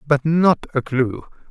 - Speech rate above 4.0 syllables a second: No, 3.6 syllables/s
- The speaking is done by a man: Yes, male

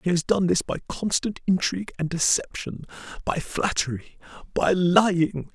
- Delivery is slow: Yes, slow, 130 wpm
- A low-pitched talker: No, medium, 180 Hz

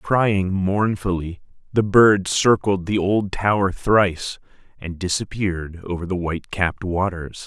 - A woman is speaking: No, male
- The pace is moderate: No, slow, 130 wpm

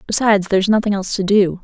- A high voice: Yes, high, 200 Hz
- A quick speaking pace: Yes, fast, 255 wpm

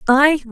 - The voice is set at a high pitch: Yes, very high, 275 Hz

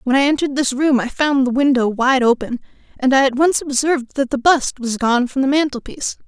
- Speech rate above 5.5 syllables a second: Yes, 5.8 syllables/s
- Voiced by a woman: Yes, female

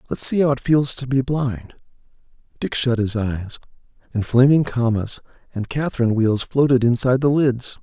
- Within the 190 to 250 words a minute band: No, average, 170 wpm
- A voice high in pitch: No, low, 125 Hz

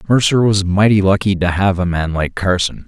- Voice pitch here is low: Yes, very low, 95 Hz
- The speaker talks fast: Yes, fast, 210 wpm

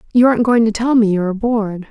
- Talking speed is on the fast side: Yes, fast, 285 wpm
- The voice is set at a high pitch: Yes, high, 220 Hz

